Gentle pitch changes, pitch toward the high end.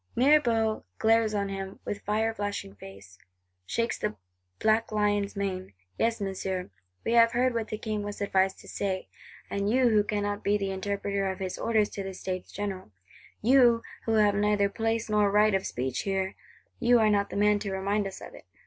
Yes: narrow, 2.3 semitones; high, 205 Hz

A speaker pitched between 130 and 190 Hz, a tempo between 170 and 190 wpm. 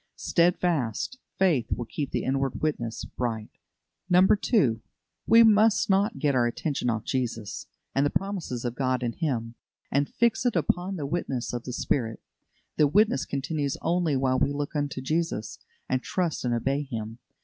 No: medium, 140 Hz; average, 160 wpm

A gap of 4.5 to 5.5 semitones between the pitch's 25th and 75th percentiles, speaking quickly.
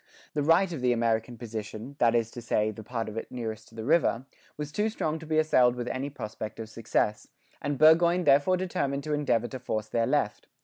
Yes: average, 5.2 semitones; fast, 220 wpm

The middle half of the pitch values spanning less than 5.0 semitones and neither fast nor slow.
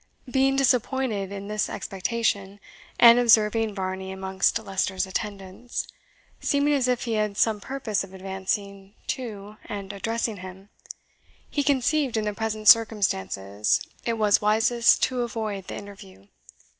No: average, 3.2 semitones; slow, 130 wpm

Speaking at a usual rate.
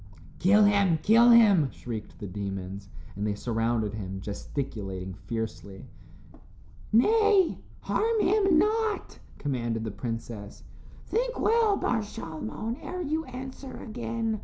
No: slow, 115 wpm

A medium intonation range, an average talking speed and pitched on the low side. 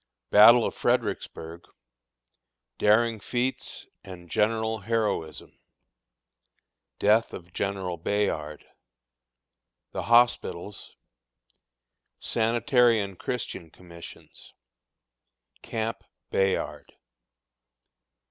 No: average, 4.3 semitones; slow, 65 wpm; low, 105 Hz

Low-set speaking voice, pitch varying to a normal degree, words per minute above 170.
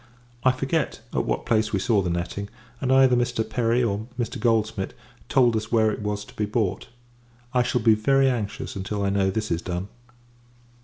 Yes: low, 110 Hz; average, 3.4 semitones; average, 195 wpm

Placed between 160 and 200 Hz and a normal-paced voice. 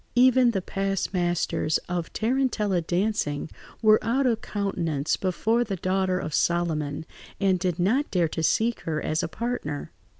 Yes: high, 190 Hz; average, 155 wpm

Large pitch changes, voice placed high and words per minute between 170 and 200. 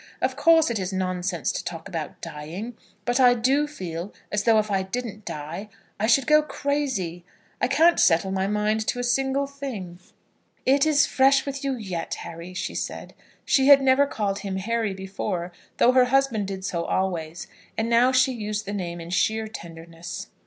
Yes: wide, 6.2 semitones; high, 215 Hz; average, 185 wpm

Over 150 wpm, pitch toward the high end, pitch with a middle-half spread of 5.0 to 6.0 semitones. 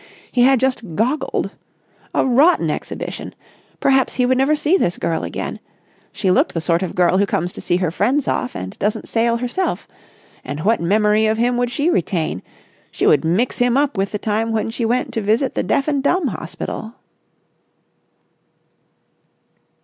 Yes: average, 170 wpm; high, 230 Hz; wide, 5.5 semitones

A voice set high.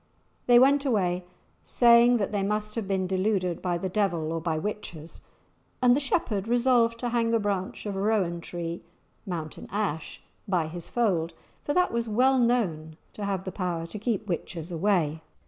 Yes: high, 200 Hz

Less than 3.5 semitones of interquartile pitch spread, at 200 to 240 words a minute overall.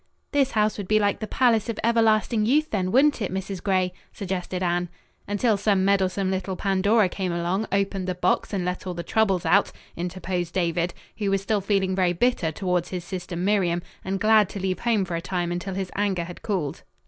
Yes: narrow, 2.6 semitones; fast, 205 wpm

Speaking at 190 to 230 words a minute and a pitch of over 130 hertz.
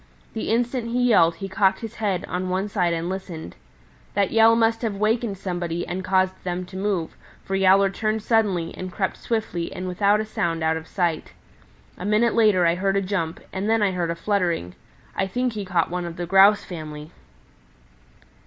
Yes: average, 195 wpm; high, 190 Hz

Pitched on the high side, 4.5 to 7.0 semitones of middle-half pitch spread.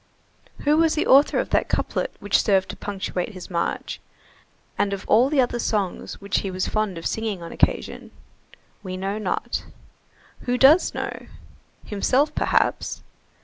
Yes: high, 210 Hz; average, 5.1 semitones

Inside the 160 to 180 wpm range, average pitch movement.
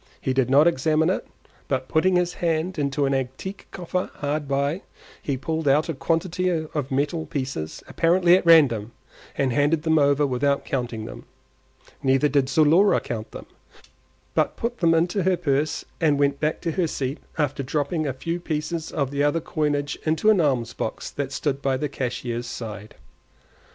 Yes: average, 175 wpm; average, 3.5 semitones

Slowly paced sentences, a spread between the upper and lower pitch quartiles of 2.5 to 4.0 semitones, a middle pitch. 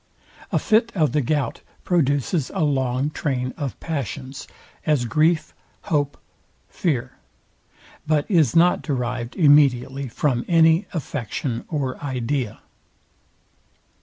Yes: slow, 105 wpm; average, 3.5 semitones; medium, 145 Hz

